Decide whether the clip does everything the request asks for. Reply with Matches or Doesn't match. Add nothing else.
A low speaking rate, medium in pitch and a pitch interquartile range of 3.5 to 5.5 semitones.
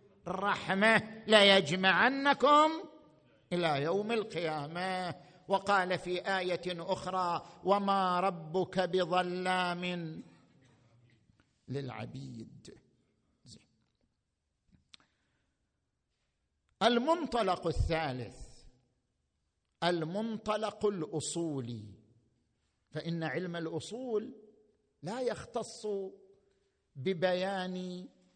Matches